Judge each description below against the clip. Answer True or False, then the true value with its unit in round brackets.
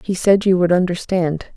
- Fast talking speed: False (190 wpm)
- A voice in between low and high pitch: True (180 Hz)